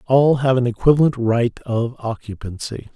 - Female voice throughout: No, male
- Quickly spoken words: No, average, 140 wpm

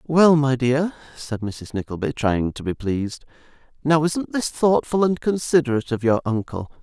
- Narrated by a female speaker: No, male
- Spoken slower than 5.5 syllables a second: Yes, 4.9 syllables/s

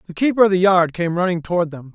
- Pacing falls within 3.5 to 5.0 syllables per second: No, 6.7 syllables/s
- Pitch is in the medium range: Yes, medium, 175 Hz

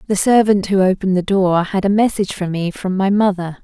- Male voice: No, female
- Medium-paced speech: No, fast, 230 wpm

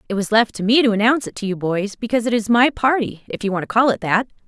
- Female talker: Yes, female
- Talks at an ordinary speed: No, fast, 310 wpm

